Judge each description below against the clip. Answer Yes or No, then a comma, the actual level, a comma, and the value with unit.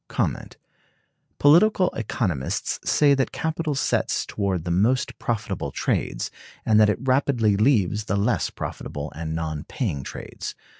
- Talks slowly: Yes, slow, 130 wpm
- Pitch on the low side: Yes, low, 105 Hz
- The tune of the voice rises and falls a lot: Yes, wide, 7.2 semitones